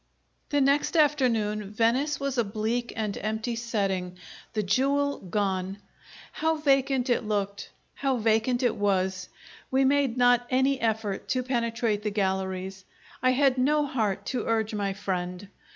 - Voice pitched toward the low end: No, high, 230 Hz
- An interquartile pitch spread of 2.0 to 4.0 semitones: No, average, 4.6 semitones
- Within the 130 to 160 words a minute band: Yes, average, 145 wpm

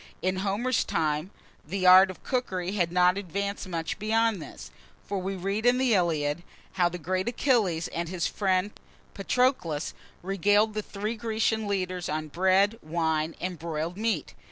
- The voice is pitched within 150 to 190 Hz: Yes, medium, 185 Hz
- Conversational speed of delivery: Yes, average, 155 wpm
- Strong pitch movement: No, average, 3.5 semitones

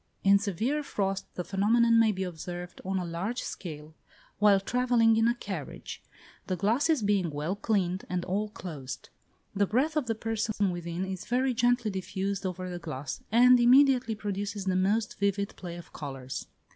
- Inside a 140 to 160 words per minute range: No, average, 170 wpm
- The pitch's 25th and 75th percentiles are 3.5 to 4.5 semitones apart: Yes, average, 4.1 semitones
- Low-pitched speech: No, high, 200 Hz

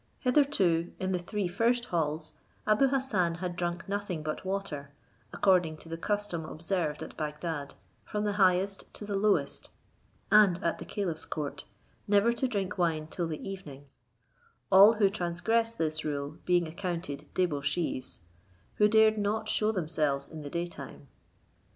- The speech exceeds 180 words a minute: No, average, 150 wpm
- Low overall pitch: No, medium, 180 Hz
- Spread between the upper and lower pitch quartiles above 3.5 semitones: Yes, average, 4.5 semitones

